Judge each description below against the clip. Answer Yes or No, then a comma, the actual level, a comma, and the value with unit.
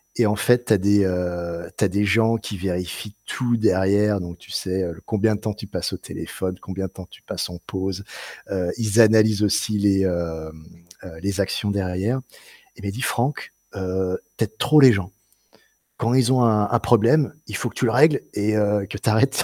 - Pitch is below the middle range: Yes, low, 100 Hz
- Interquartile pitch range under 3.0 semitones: No, average, 3.3 semitones